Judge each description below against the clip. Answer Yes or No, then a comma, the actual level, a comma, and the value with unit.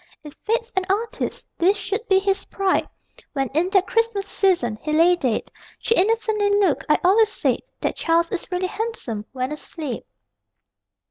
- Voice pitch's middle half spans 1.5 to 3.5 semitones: No, average, 4.7 semitones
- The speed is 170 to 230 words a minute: No, average, 160 wpm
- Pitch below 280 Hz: No, very high, 380 Hz